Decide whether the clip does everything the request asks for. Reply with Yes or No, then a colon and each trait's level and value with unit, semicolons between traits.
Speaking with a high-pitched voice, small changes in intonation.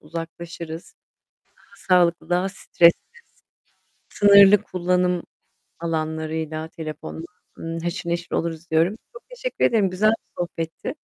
No: medium, 170 Hz; narrow, 2.2 semitones